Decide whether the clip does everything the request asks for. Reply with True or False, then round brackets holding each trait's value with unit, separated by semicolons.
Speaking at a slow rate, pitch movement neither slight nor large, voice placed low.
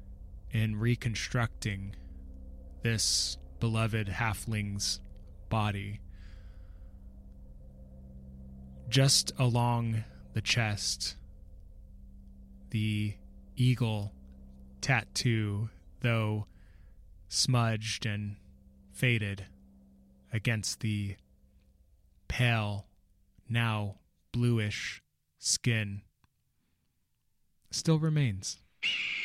False (50 wpm; 8.3 semitones; 100 Hz)